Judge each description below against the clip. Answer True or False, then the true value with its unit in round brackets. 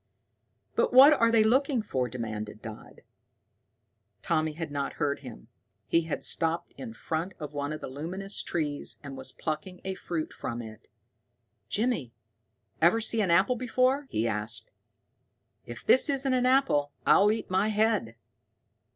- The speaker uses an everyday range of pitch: False (8.1 semitones)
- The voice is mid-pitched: True (170 Hz)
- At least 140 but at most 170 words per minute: True (150 wpm)